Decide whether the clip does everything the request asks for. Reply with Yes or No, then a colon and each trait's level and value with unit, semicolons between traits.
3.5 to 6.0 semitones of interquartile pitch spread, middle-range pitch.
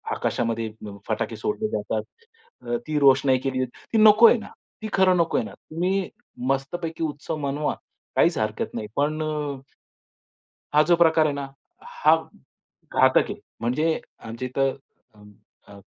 Yes: average, 4.2 semitones; medium, 150 Hz